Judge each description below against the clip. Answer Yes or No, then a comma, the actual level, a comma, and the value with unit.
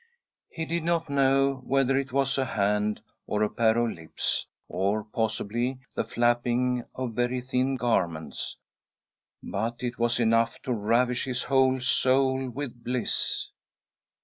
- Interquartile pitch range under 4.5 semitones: Yes, narrow, 2.6 semitones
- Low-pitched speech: Yes, low, 125 Hz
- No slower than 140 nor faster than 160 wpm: Yes, average, 145 wpm